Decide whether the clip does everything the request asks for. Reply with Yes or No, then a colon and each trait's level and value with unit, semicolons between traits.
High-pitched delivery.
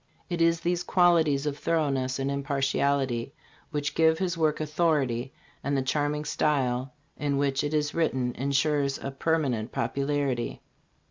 No: medium, 145 Hz